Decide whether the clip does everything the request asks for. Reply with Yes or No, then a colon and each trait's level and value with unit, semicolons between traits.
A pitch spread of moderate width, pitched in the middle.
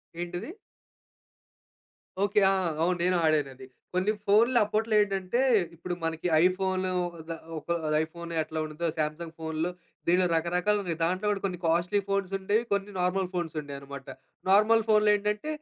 Yes: average, 3.7 semitones; medium, 180 Hz